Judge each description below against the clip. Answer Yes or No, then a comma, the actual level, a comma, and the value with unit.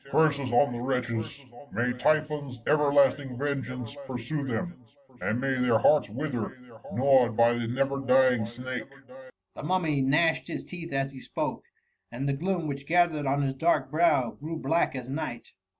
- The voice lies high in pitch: No, low, 135 Hz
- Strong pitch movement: No, average, 3.2 semitones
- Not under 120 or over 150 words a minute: No, average, 170 wpm